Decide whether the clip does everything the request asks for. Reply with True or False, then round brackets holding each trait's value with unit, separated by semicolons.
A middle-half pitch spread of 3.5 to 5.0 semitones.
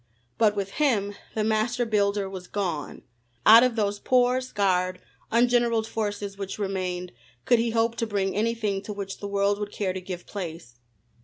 False (2.7 semitones)